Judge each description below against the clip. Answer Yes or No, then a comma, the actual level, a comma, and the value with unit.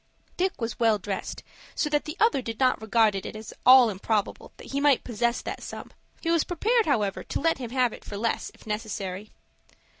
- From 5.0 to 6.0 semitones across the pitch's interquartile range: Yes, wide, 5.4 semitones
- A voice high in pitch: Yes, high, 235 Hz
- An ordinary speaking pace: No, fast, 210 wpm